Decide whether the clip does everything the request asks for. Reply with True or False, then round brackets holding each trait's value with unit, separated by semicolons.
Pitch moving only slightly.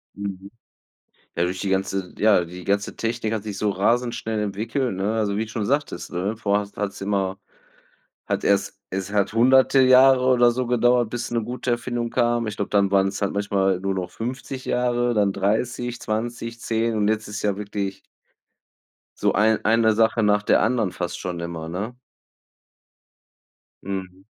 False (3.3 semitones)